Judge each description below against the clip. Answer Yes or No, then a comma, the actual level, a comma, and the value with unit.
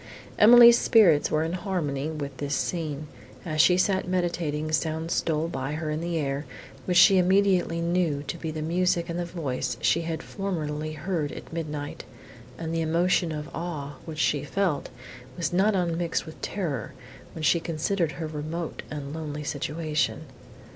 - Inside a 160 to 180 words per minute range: Yes, average, 165 wpm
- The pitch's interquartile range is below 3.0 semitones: Yes, narrow, 2.6 semitones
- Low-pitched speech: No, medium, 160 Hz